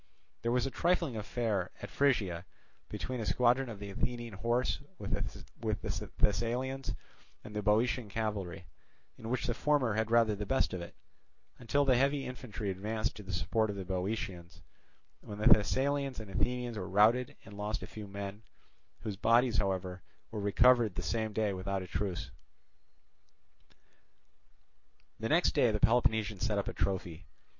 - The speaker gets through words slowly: No, average, 160 wpm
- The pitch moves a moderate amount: Yes, average, 3.7 semitones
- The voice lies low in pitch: Yes, low, 110 Hz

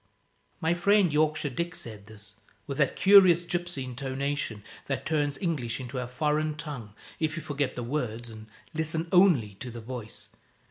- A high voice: No, medium, 145 Hz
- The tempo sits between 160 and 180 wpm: Yes, average, 165 wpm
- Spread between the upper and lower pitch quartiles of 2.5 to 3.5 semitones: No, average, 4.7 semitones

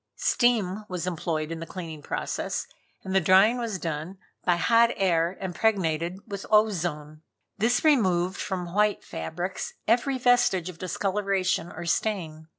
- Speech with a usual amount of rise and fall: Yes, average, 4.0 semitones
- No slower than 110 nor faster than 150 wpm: Yes, average, 140 wpm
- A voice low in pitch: No, medium, 185 Hz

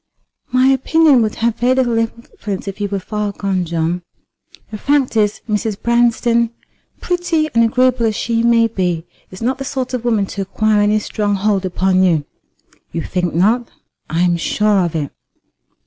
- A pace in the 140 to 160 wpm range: No, average, 175 wpm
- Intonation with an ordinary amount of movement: Yes, average, 3.9 semitones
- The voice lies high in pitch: Yes, high, 215 Hz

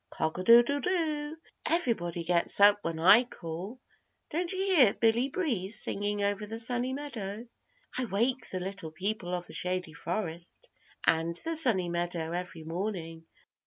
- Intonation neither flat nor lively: No, wide, 6.3 semitones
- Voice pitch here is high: Yes, high, 205 Hz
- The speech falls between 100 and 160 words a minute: Yes, average, 155 wpm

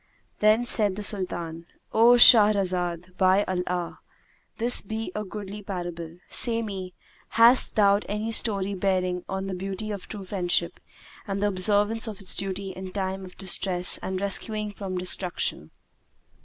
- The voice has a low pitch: No, high, 195 Hz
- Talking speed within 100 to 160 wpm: Yes, average, 145 wpm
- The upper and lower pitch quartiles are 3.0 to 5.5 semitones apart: No, narrow, 2.4 semitones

